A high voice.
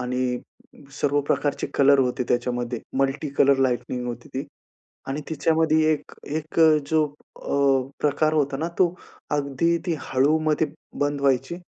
No: medium, 140 Hz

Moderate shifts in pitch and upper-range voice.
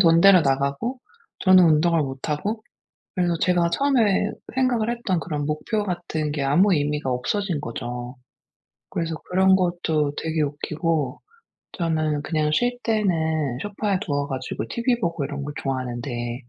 No: average, 4.9 semitones; medium, 160 Hz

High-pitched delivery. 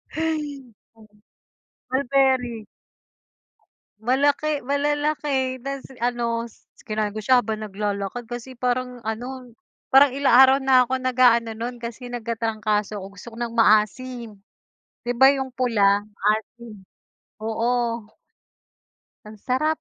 Yes: high, 245 Hz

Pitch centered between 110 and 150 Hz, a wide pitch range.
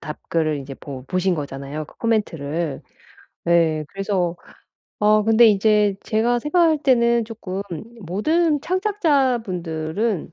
No: high, 200 Hz; wide, 6.7 semitones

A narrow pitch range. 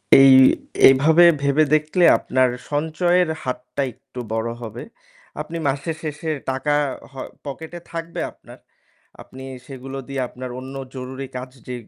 No: average, 3.3 semitones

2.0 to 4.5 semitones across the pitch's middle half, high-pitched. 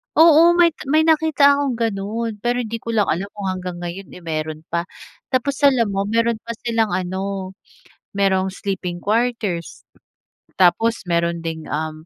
No: average, 4.9 semitones; high, 200 Hz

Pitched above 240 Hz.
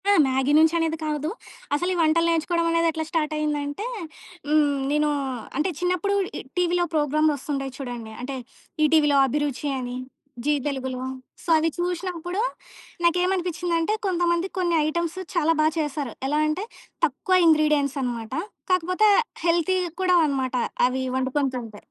Yes: very high, 310 Hz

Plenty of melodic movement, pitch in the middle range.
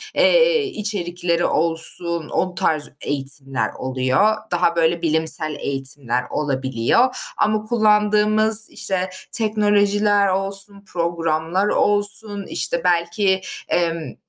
No: average, 4.6 semitones; medium, 180 Hz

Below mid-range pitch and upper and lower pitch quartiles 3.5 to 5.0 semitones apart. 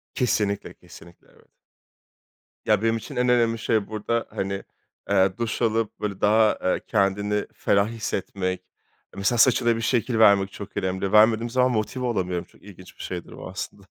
No: low, 105 Hz; average, 2.8 semitones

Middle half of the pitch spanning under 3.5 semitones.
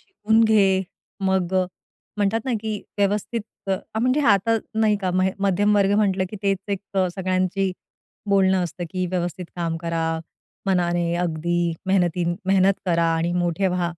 Yes: narrow, 2.5 semitones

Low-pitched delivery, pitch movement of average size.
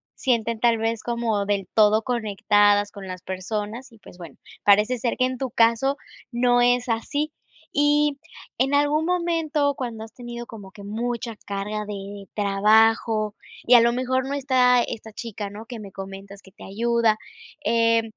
No: high, 230 Hz; average, 3.2 semitones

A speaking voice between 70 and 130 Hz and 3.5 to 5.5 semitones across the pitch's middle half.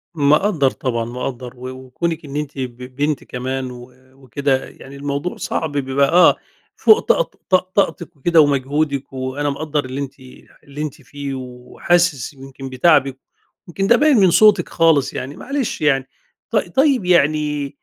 No: medium, 140 Hz; average, 4.2 semitones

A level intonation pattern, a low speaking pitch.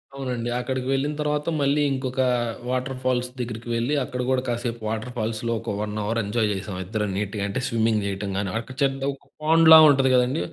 No: average, 3.5 semitones; low, 125 Hz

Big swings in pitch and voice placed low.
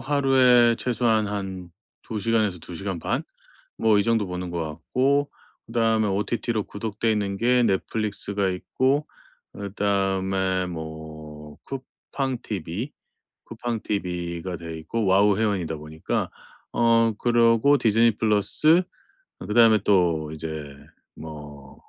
No: average, 4.7 semitones; low, 105 Hz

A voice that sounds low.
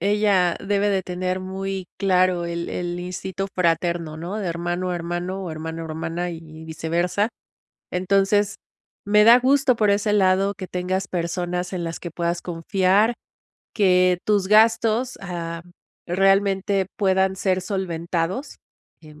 No: medium, 185 Hz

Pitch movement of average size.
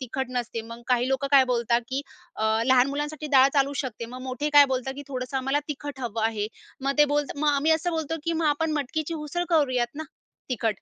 Yes: average, 3.0 semitones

